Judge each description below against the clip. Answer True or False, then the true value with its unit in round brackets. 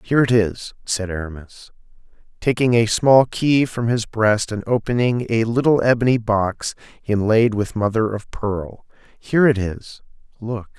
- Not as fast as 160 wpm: True (150 wpm)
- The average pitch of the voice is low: True (110 Hz)